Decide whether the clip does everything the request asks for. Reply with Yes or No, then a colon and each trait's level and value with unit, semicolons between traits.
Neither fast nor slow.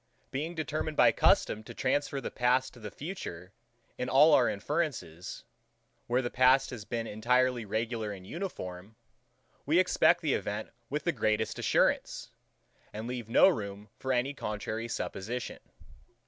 Yes: average, 145 wpm